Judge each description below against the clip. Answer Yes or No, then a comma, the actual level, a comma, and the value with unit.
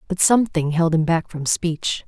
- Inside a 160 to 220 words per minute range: Yes, fast, 205 wpm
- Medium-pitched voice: Yes, medium, 170 Hz